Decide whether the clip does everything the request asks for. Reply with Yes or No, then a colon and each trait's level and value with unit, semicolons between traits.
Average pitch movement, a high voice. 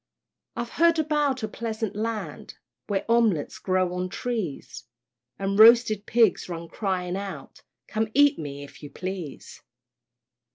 Yes: average, 4.4 semitones; high, 210 Hz